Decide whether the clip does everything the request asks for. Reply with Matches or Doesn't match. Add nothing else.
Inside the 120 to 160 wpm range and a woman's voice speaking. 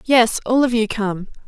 Doesn't match